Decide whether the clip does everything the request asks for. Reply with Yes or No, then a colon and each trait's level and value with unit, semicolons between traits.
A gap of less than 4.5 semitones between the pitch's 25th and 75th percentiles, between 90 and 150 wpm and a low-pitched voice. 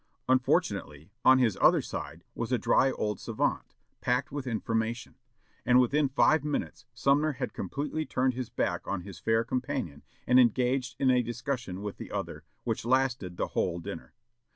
No: average, 3.2 semitones; average, 165 wpm; low, 125 Hz